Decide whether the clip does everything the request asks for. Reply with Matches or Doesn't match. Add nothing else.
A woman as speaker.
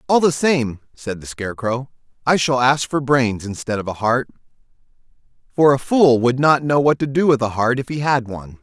Doesn't match